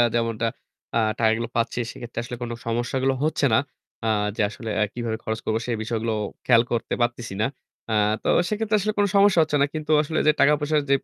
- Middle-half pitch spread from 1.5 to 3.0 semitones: No, average, 4.8 semitones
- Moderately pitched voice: No, low, 120 Hz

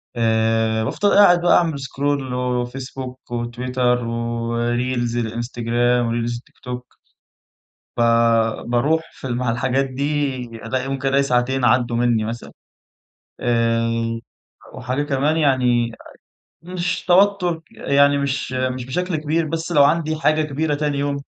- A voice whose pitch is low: Yes, low, 125 Hz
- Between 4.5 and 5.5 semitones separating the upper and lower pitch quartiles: No, average, 3.3 semitones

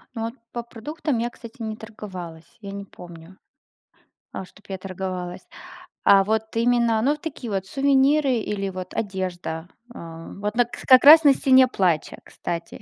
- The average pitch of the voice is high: Yes, high, 215 Hz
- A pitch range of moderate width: Yes, average, 4.9 semitones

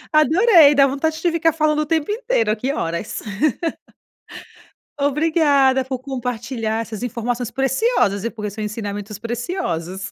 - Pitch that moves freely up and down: Yes, wide, 5.8 semitones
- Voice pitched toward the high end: Yes, very high, 260 Hz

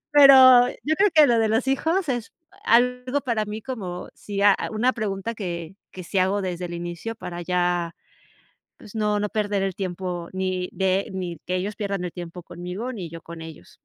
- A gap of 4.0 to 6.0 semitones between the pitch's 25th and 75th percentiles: Yes, average, 4.5 semitones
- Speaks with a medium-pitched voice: No, high, 195 Hz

